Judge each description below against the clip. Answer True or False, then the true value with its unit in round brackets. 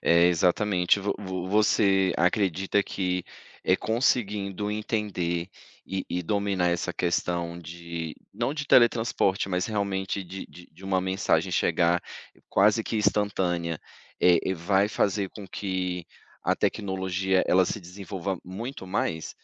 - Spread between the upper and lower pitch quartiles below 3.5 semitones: True (2.4 semitones)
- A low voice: True (95 Hz)